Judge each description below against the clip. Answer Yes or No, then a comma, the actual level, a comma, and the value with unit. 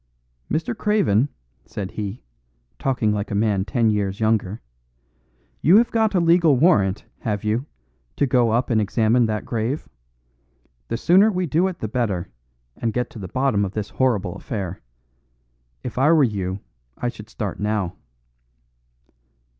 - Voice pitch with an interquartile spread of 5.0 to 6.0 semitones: Yes, average, 5.3 semitones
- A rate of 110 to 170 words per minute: Yes, average, 155 wpm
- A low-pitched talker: Yes, low, 115 Hz